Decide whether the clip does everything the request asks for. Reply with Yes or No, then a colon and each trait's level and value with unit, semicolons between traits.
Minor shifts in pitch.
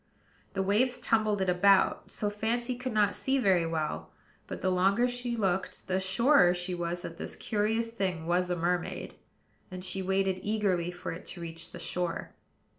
No: average, 3.7 semitones